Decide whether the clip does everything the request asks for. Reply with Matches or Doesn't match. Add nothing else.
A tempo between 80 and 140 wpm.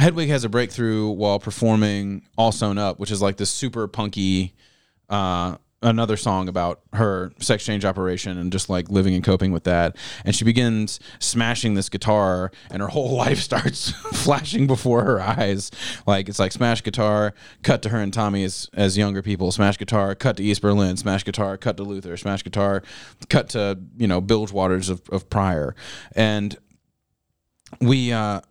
Doesn't match